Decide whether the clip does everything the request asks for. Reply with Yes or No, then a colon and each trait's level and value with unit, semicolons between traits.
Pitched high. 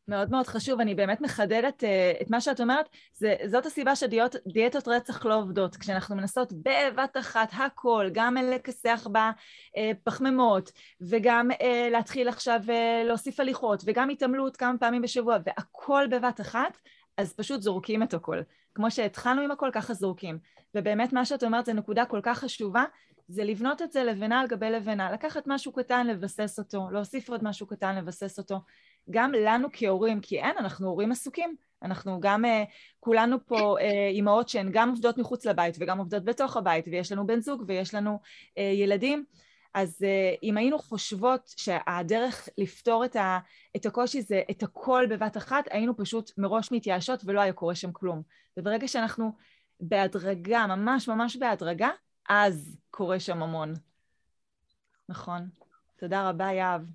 Yes: high, 225 Hz